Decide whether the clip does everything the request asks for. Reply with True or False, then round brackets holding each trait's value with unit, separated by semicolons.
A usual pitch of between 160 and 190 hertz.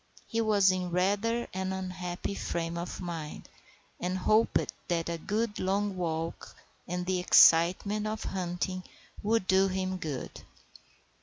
True (185 Hz)